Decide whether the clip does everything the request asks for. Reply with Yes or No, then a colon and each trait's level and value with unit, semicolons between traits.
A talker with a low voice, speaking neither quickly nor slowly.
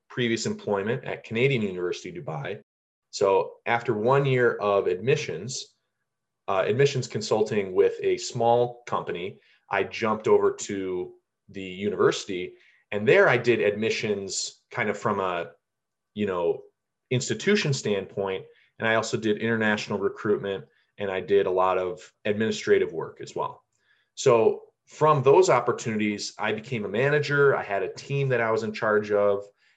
No: medium, 150 Hz; average, 145 wpm